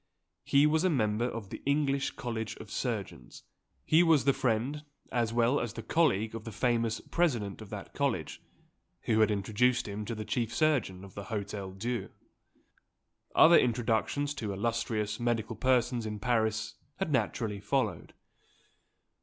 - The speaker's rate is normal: Yes, average, 155 wpm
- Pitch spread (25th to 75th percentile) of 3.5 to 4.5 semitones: Yes, average, 3.8 semitones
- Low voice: Yes, low, 115 Hz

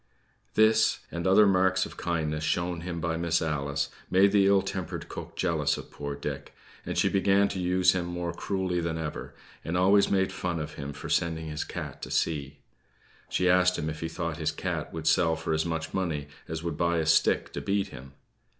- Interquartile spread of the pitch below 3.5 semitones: Yes, average, 2.7 semitones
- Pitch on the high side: No, very low, 85 Hz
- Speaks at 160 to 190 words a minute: No, fast, 205 wpm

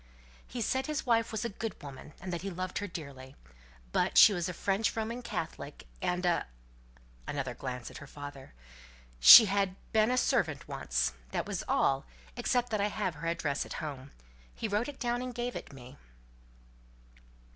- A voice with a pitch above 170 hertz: Yes, medium, 185 Hz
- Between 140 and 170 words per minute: No, average, 180 wpm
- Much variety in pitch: Yes, wide, 8.0 semitones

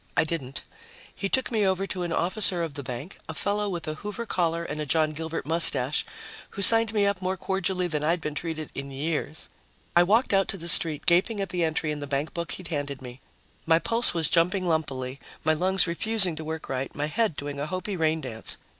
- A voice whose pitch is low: No, medium, 165 Hz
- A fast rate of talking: Yes, fast, 220 wpm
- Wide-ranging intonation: No, average, 3.9 semitones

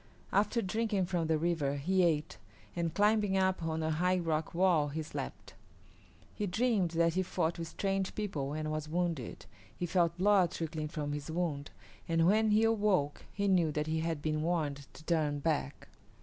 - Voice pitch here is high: No, medium, 170 Hz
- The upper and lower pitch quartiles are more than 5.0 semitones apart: No, average, 3.5 semitones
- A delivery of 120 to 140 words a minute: No, average, 180 wpm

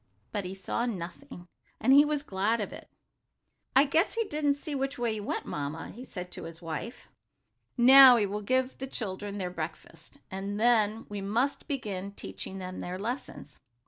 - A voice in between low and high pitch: No, high, 215 Hz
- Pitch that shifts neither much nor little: No, wide, 5.8 semitones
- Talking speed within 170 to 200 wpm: Yes, average, 180 wpm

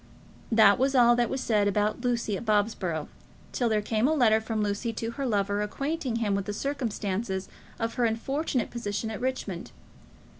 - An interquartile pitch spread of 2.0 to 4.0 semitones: Yes, average, 3.0 semitones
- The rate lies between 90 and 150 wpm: No, average, 180 wpm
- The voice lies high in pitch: Yes, high, 225 Hz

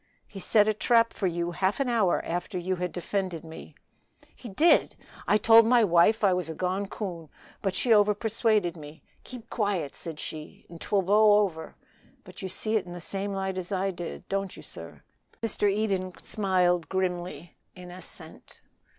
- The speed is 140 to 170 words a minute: No, average, 180 wpm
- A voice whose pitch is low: No, high, 190 Hz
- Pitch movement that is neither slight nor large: Yes, average, 3.1 semitones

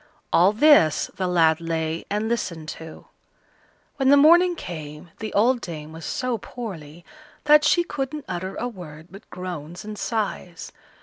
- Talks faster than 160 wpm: No, average, 150 wpm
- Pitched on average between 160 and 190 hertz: Yes, medium, 185 Hz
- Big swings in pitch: Yes, wide, 7.1 semitones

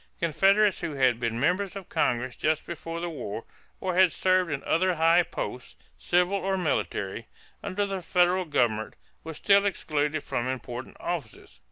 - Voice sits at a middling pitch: Yes, medium, 165 Hz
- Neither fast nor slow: Yes, average, 160 wpm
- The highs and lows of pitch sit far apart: Yes, wide, 6.4 semitones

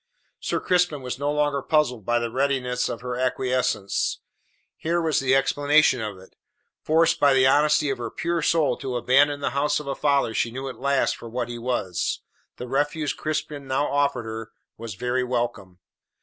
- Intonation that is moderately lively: Yes, average, 3.2 semitones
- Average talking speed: Yes, average, 185 wpm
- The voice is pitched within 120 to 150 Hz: Yes, low, 135 Hz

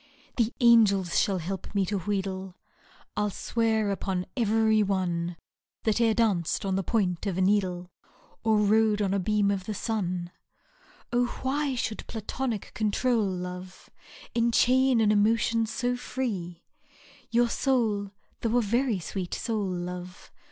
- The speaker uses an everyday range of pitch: Yes, average, 3.6 semitones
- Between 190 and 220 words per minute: No, average, 155 wpm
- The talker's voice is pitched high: Yes, high, 210 Hz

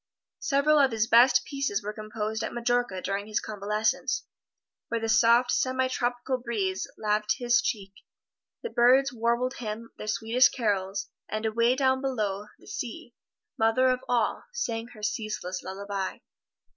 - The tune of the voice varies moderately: Yes, average, 3.0 semitones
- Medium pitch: No, high, 230 Hz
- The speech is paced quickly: No, average, 145 wpm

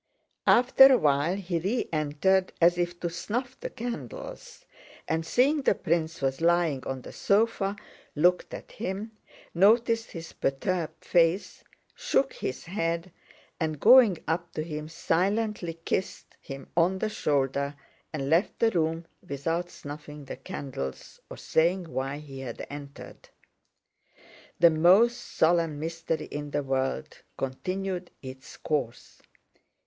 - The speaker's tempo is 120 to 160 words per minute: Yes, slow, 135 wpm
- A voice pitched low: No, medium, 165 Hz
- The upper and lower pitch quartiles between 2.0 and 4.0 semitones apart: No, average, 4.6 semitones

